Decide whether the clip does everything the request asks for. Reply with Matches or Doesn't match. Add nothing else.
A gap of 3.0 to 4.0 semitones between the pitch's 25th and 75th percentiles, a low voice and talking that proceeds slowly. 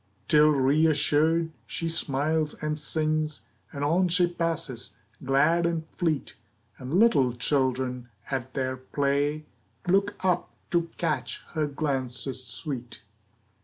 Doesn't match